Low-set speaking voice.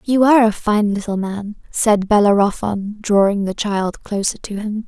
No: high, 210 Hz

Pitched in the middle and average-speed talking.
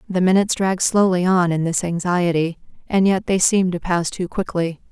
Yes: medium, 180 Hz; average, 195 wpm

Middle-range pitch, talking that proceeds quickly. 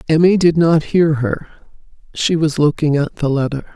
No: medium, 155 Hz; average, 175 wpm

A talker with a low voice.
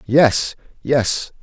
Yes: low, 130 Hz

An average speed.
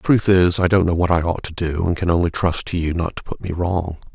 No: fast, 320 wpm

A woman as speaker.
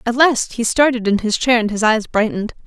Yes: female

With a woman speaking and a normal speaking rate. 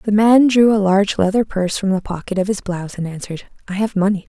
No: female; fast, 250 wpm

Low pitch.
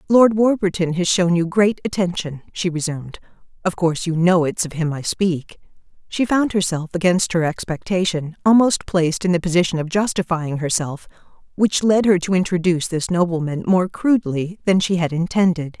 No: medium, 175 Hz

